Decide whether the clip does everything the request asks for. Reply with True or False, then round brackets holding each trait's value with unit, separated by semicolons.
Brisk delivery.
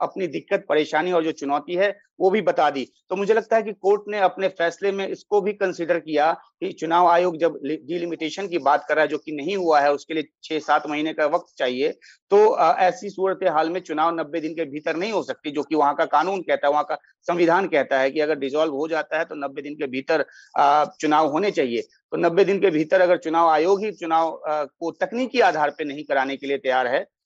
True (240 wpm)